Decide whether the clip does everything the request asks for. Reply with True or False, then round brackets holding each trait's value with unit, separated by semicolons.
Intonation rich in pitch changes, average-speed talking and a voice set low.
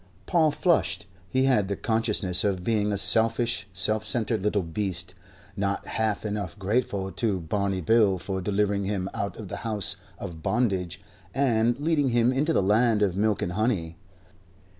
False (3.2 semitones; 160 wpm; 105 Hz)